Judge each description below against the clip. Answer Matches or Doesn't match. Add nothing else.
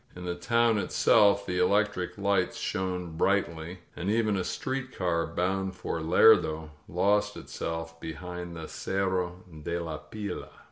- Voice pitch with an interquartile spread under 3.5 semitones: Matches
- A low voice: Matches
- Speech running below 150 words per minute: Matches